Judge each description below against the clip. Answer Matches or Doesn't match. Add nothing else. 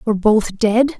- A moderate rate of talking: Matches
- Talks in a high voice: Matches